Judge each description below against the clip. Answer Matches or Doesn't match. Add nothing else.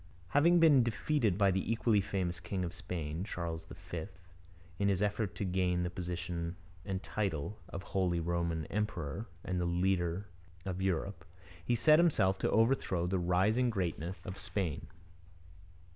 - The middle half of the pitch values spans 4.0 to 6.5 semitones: Doesn't match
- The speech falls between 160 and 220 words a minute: Doesn't match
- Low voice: Matches